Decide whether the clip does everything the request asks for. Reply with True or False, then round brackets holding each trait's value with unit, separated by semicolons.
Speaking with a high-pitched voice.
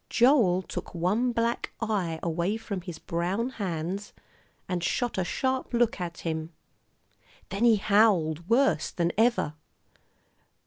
True (195 Hz)